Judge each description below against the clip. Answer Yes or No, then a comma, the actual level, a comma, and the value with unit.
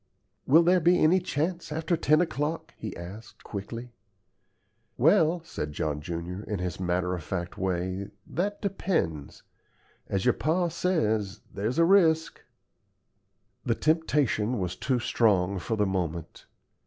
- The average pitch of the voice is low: Yes, low, 115 Hz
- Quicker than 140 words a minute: No, slow, 135 wpm